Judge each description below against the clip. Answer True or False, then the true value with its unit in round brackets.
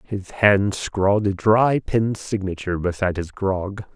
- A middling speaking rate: True (150 wpm)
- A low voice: True (100 Hz)